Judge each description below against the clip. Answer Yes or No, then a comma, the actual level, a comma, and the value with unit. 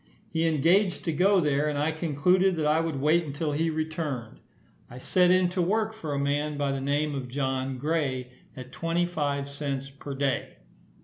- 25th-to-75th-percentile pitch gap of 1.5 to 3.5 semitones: Yes, average, 3.1 semitones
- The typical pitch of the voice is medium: Yes, medium, 150 Hz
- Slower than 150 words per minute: No, average, 190 wpm